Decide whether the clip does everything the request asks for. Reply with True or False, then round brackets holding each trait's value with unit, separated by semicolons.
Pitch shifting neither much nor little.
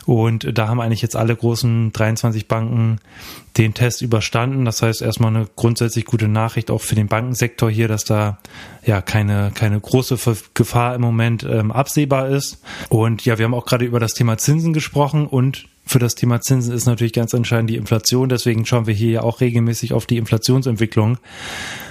False (1.6 semitones)